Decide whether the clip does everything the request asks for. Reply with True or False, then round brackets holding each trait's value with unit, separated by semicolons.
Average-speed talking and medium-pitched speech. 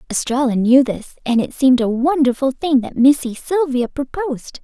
False (170 wpm; 265 Hz)